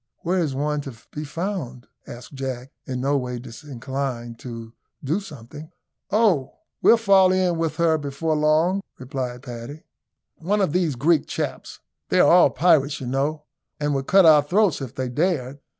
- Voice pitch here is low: No, medium, 145 Hz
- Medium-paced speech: Yes, average, 165 wpm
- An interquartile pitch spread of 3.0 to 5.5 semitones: Yes, average, 4.5 semitones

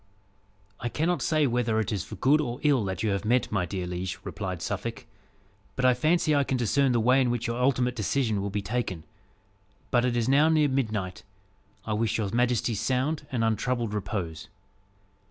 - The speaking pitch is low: Yes, low, 120 Hz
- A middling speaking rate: Yes, average, 190 wpm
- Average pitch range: Yes, average, 4.1 semitones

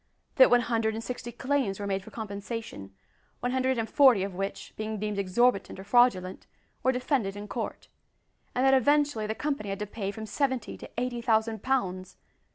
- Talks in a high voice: Yes, high, 225 Hz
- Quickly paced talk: No, average, 185 wpm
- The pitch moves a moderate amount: Yes, average, 3.9 semitones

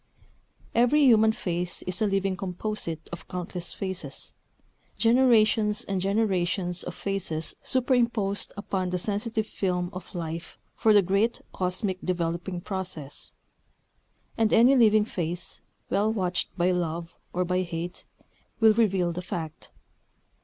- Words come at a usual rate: No, slow, 125 wpm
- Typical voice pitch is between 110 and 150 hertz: No, high, 190 Hz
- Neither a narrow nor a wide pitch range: Yes, average, 3.4 semitones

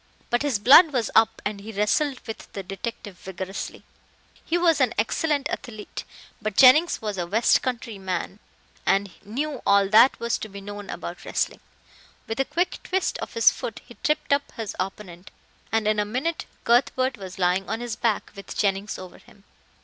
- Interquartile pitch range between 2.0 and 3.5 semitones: No, average, 4.5 semitones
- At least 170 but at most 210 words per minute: Yes, average, 180 wpm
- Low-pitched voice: No, high, 220 Hz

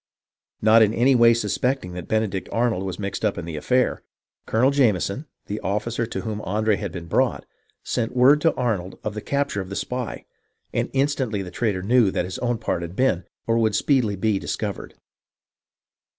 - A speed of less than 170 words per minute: No, average, 185 wpm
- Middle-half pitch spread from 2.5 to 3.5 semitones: No, average, 4.2 semitones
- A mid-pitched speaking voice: No, low, 110 Hz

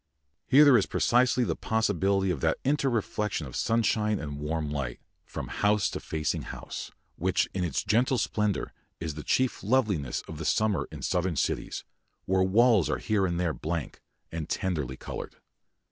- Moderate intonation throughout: No, wide, 5.9 semitones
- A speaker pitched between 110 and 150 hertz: No, very low, 95 Hz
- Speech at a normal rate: Yes, average, 165 wpm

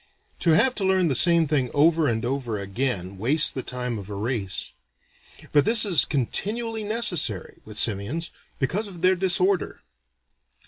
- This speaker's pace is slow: No, average, 155 wpm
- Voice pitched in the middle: Yes, medium, 150 Hz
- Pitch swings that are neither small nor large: No, wide, 8.0 semitones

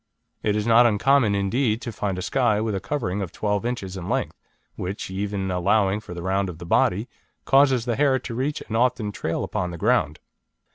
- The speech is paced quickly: Yes, fast, 210 wpm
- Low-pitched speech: Yes, low, 105 Hz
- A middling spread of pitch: Yes, average, 4.2 semitones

